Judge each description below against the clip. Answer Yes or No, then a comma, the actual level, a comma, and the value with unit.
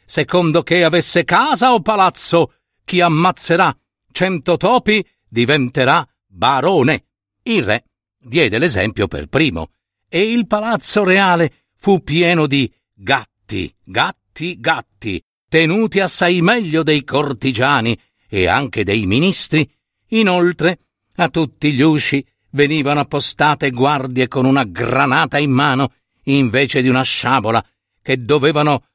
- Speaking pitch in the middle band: Yes, medium, 145 Hz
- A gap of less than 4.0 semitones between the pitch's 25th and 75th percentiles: No, average, 5.1 semitones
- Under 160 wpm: Yes, slow, 115 wpm